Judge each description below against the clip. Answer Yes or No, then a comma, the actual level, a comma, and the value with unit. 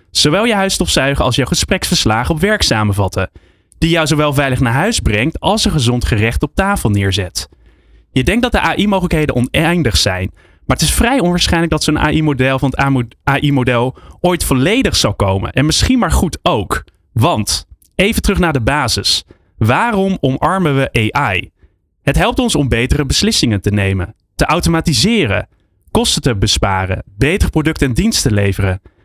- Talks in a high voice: No, low, 130 Hz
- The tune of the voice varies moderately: No, wide, 8.6 semitones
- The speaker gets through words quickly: No, average, 165 wpm